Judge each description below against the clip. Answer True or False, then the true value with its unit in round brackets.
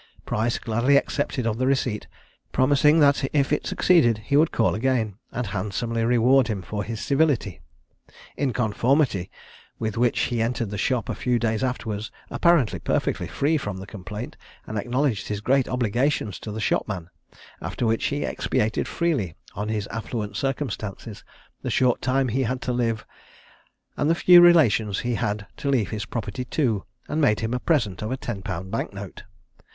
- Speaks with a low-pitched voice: True (115 Hz)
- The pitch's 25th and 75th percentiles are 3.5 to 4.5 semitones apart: True (4.1 semitones)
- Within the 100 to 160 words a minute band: False (175 wpm)